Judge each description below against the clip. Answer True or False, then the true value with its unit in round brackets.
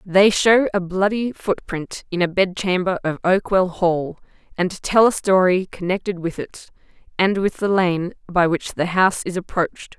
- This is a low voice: False (185 Hz)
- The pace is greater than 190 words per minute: False (175 wpm)